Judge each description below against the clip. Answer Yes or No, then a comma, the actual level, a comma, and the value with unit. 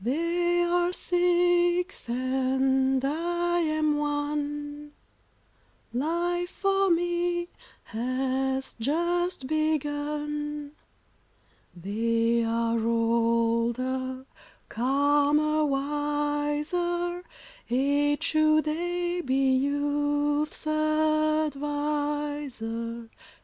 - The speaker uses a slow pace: Yes, slow, 60 wpm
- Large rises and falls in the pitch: No, average, 3.8 semitones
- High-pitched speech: Yes, very high, 295 Hz